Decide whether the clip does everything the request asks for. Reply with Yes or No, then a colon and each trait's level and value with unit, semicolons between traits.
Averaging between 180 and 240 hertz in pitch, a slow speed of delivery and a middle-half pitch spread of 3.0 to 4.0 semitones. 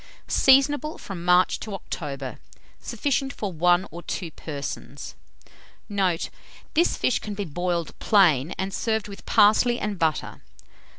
No: high, 190 Hz; slow, 130 wpm; average, 4.5 semitones